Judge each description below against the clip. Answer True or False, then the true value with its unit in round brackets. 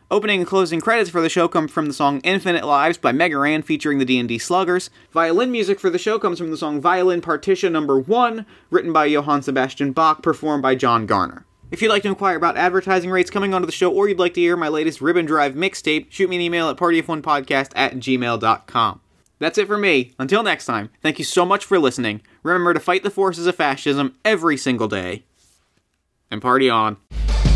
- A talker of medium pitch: True (165 Hz)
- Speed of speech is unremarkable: False (215 wpm)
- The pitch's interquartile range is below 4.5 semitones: False (5.2 semitones)